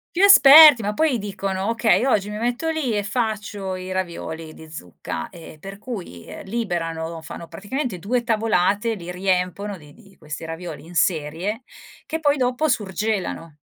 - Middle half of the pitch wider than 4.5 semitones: Yes, wide, 5.6 semitones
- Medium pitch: No, high, 200 Hz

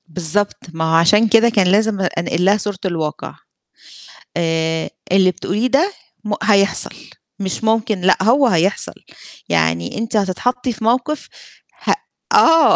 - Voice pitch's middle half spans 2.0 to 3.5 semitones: No, average, 4.9 semitones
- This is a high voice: Yes, high, 200 Hz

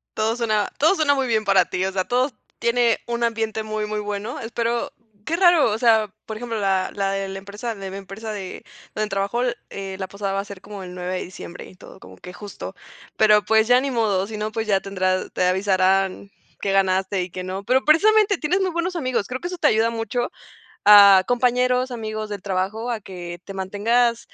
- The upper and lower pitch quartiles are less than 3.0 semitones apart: No, average, 3.5 semitones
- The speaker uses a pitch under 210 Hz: No, high, 215 Hz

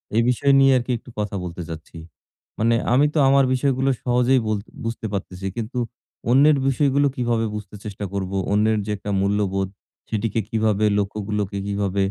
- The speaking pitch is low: Yes, low, 110 Hz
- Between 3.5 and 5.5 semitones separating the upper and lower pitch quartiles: Yes, average, 3.8 semitones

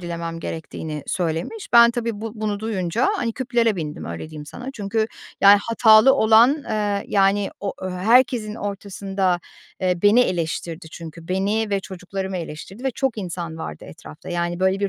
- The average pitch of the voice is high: Yes, high, 195 Hz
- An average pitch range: Yes, average, 4.3 semitones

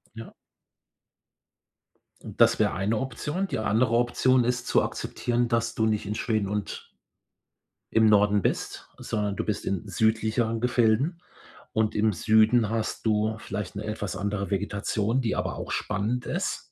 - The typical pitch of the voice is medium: No, low, 110 Hz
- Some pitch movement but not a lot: No, narrow, 2.2 semitones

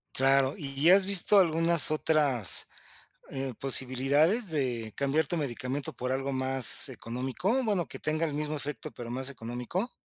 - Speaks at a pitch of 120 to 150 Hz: Yes, medium, 140 Hz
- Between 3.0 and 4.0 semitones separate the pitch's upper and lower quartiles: Yes, average, 3.7 semitones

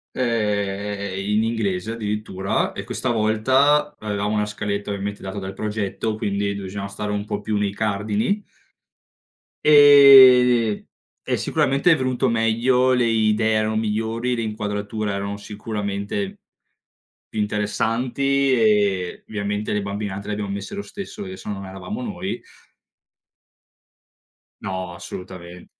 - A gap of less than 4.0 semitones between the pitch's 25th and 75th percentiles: Yes, average, 2.9 semitones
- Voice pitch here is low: Yes, low, 105 Hz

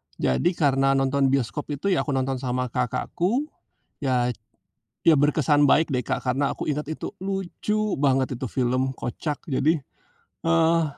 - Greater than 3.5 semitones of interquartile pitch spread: Yes, average, 3.9 semitones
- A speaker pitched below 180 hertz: Yes, medium, 140 Hz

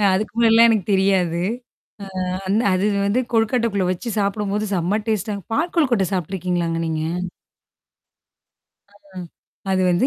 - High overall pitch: Yes, high, 200 Hz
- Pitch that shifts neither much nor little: Yes, average, 3.3 semitones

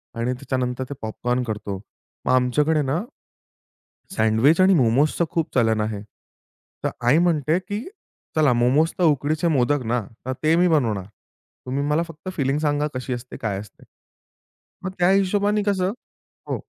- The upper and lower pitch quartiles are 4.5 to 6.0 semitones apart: Yes, average, 5.1 semitones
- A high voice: No, medium, 145 Hz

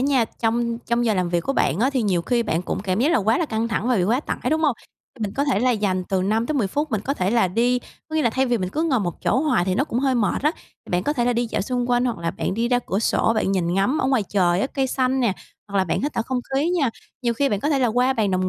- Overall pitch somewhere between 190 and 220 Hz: No, high, 235 Hz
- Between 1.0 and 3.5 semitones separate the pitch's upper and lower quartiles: No, average, 5.1 semitones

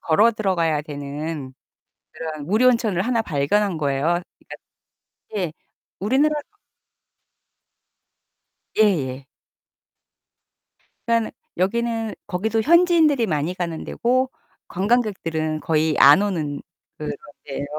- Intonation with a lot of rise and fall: Yes, wide, 6.7 semitones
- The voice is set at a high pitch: No, medium, 180 Hz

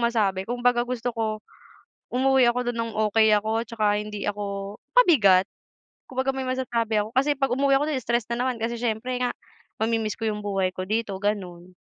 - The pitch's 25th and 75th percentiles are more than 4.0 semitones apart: No, average, 3.1 semitones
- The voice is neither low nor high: No, high, 230 Hz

